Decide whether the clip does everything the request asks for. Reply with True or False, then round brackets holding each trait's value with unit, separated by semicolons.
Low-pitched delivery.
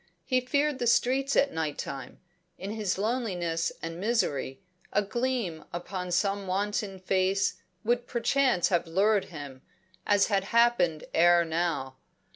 False (195 Hz)